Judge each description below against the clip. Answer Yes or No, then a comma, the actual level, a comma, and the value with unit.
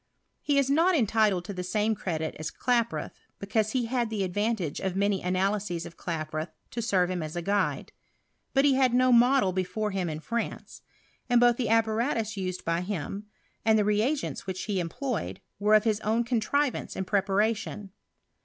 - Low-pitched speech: No, high, 210 Hz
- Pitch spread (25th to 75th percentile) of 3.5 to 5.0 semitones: Yes, average, 4.1 semitones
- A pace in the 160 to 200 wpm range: Yes, average, 180 wpm